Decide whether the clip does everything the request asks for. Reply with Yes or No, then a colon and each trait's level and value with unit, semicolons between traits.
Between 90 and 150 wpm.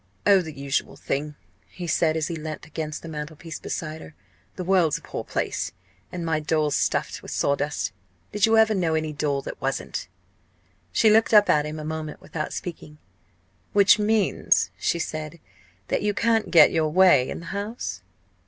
No: average, 180 wpm